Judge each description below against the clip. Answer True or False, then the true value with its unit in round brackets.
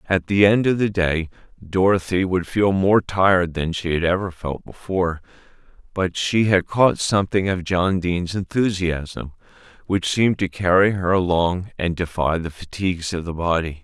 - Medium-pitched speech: False (90 Hz)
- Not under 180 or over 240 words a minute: False (170 wpm)